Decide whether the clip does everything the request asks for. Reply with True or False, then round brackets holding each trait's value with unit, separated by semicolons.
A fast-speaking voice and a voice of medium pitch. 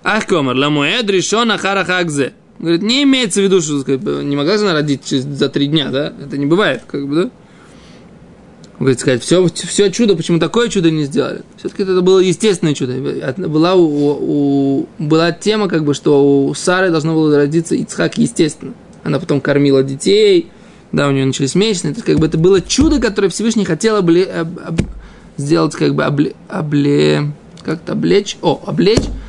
True (180 wpm; 165 Hz)